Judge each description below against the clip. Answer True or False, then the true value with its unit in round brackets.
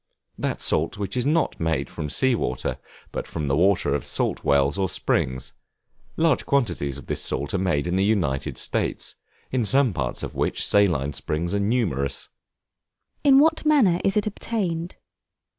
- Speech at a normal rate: True (170 wpm)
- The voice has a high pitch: False (100 Hz)